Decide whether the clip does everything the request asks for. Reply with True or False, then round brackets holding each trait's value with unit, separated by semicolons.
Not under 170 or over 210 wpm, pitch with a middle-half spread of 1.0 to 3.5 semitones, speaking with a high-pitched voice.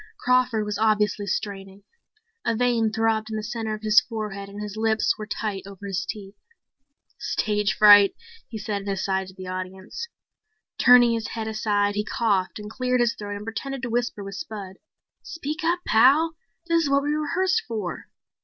True (180 wpm; 3.1 semitones; 215 Hz)